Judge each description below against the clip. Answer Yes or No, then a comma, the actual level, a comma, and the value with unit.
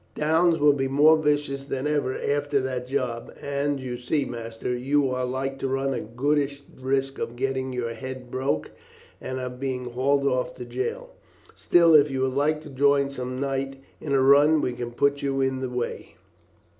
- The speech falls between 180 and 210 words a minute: Yes, average, 190 wpm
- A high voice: No, low, 135 Hz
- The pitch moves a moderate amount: No, narrow, 1.9 semitones